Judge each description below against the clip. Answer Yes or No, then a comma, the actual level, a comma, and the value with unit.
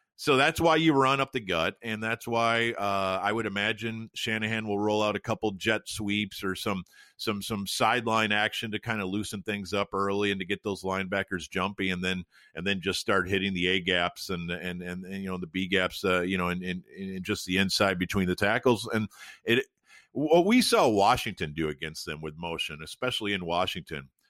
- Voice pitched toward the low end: Yes, low, 100 Hz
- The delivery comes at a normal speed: No, fast, 215 wpm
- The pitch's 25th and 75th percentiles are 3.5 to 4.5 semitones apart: No, average, 3.1 semitones